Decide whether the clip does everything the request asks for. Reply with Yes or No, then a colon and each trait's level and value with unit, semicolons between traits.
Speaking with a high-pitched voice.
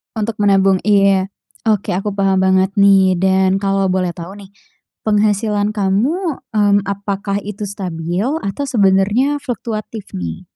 Yes: high, 200 Hz